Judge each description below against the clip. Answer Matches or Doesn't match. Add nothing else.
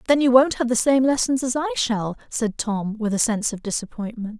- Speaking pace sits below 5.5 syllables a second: Doesn't match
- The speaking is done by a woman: Matches